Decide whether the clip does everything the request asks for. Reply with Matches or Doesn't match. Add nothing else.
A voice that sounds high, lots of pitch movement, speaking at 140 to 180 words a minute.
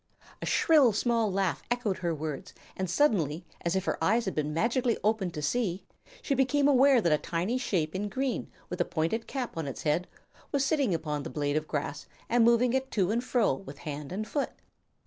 Doesn't match